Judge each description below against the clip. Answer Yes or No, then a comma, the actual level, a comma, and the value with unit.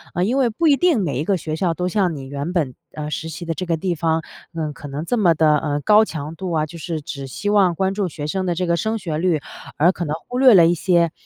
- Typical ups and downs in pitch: Yes, average, 3.6 semitones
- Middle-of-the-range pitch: Yes, medium, 170 Hz